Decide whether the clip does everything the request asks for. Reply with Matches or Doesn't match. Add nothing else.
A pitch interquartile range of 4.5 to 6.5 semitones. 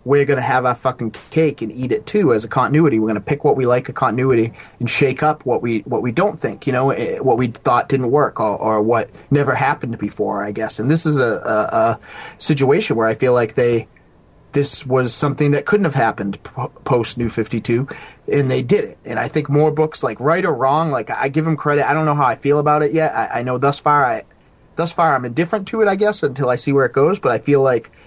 Doesn't match